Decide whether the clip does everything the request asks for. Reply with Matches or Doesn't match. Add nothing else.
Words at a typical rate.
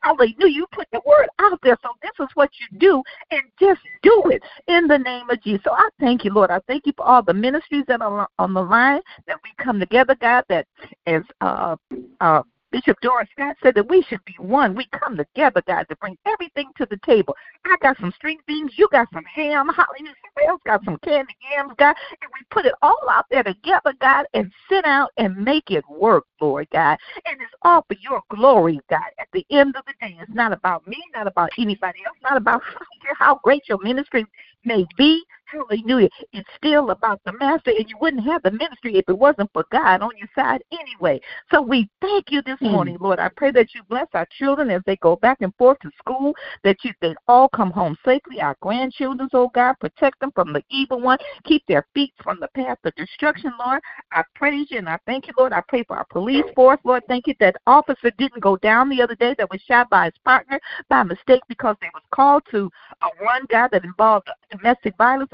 Doesn't match